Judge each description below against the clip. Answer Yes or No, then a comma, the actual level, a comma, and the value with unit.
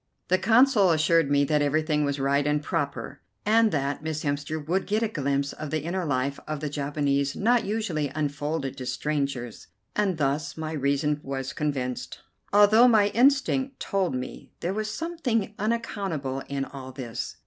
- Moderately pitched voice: Yes, medium, 150 Hz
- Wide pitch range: Yes, wide, 6.2 semitones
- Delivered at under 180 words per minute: Yes, average, 165 wpm